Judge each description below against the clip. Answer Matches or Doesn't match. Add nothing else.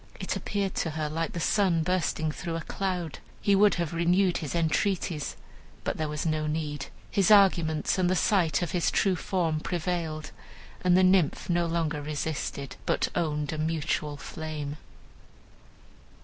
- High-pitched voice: Doesn't match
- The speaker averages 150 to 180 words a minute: Matches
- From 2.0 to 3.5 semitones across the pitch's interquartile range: Matches